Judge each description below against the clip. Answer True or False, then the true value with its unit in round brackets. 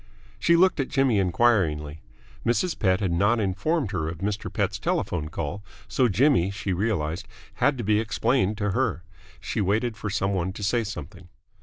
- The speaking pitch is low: True (100 Hz)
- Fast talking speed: False (175 wpm)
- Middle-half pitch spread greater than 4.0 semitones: True (4.4 semitones)